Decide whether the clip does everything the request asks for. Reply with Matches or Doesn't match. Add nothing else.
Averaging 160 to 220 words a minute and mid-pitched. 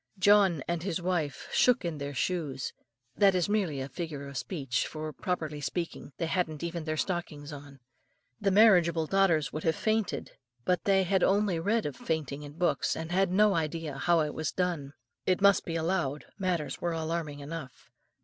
Matches